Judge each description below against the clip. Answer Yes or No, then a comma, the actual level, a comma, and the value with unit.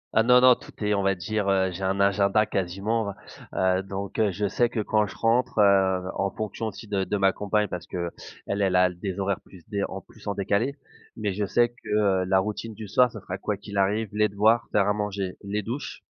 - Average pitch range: No, narrow, 2.0 semitones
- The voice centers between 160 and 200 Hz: No, low, 100 Hz